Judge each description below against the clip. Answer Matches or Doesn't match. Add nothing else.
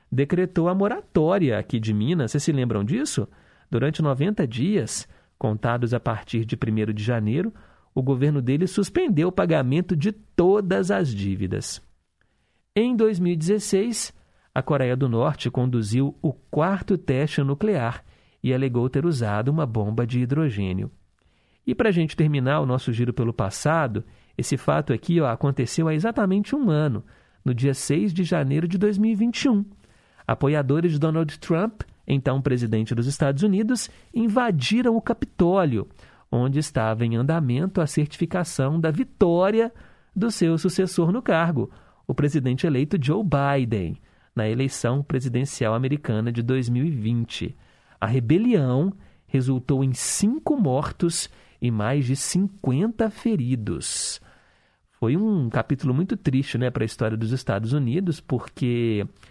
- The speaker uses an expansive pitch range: Matches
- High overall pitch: Doesn't match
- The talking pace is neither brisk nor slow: Matches